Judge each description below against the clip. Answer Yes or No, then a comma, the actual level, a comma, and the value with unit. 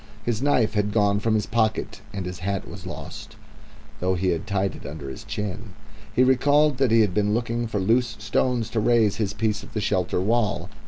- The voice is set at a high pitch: No, low, 105 Hz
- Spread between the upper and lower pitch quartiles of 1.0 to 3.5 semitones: Yes, average, 2.9 semitones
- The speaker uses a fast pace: Yes, fast, 210 wpm